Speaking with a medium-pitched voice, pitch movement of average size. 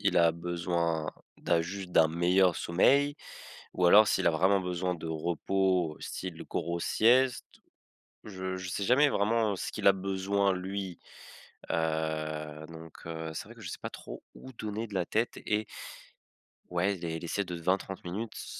No: very low, 90 Hz; average, 3.2 semitones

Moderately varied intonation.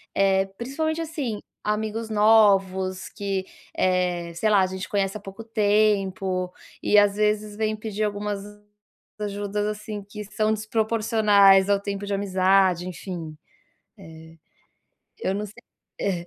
No: narrow, 1.9 semitones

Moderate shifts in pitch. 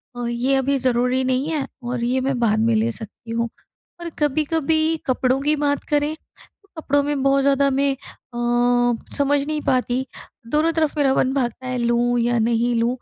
Yes: average, 3.0 semitones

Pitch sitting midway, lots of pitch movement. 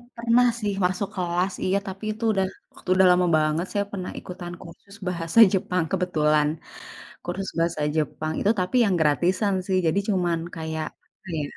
No: medium, 180 Hz; average, 2.7 semitones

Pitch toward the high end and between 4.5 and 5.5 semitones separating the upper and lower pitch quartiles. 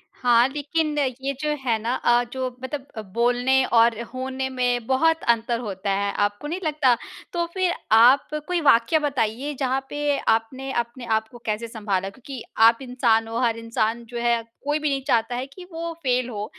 No: high, 245 Hz; average, 3.4 semitones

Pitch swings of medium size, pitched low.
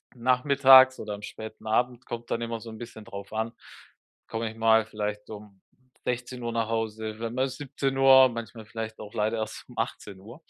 No: narrow, 2.3 semitones; low, 115 Hz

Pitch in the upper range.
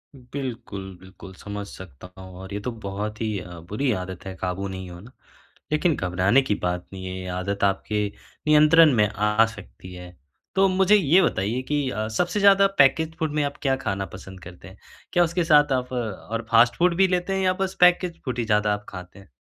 No: low, 110 Hz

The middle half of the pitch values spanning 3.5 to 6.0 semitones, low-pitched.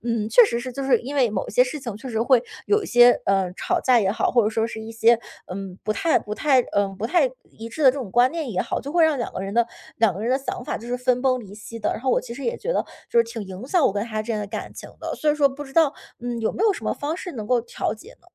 No: average, 4.0 semitones; high, 240 Hz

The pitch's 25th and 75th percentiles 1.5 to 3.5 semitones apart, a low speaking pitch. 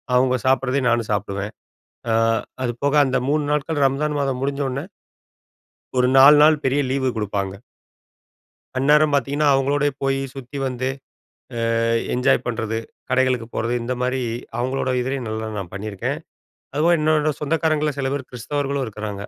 Yes: average, 3.0 semitones; low, 130 Hz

